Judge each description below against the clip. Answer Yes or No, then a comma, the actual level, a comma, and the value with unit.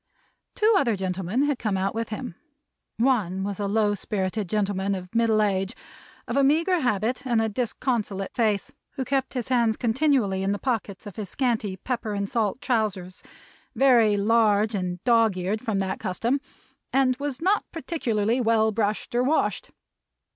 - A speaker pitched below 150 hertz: No, high, 220 Hz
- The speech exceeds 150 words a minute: Yes, average, 165 wpm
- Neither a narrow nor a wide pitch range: Yes, average, 4.0 semitones